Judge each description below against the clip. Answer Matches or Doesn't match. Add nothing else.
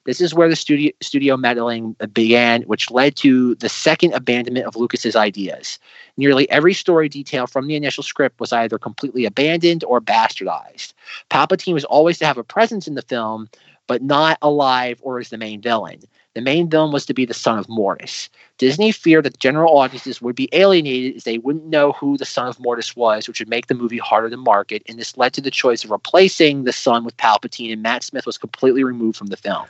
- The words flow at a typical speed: Doesn't match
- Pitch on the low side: Matches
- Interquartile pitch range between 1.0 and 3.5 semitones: Doesn't match